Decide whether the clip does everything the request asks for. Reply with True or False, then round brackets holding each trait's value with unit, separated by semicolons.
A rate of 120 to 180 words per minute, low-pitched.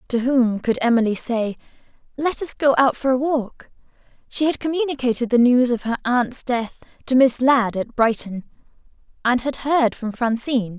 False (170 wpm; 250 Hz)